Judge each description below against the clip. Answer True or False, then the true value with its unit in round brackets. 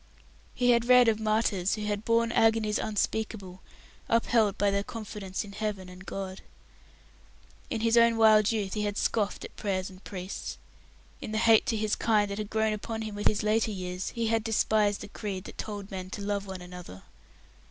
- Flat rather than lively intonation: True (2.0 semitones)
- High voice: True (210 Hz)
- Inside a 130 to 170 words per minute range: False (195 wpm)